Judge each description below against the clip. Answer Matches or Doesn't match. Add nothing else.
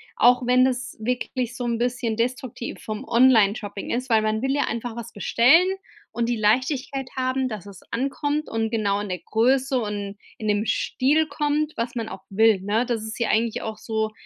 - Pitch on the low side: Doesn't match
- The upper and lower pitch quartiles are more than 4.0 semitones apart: Doesn't match